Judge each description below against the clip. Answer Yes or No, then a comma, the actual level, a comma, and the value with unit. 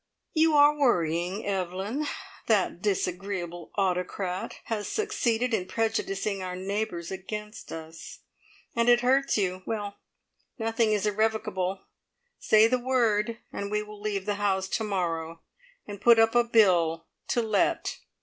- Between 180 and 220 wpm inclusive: No, slow, 135 wpm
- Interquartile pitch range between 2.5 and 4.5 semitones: Yes, average, 3.4 semitones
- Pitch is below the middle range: No, high, 205 Hz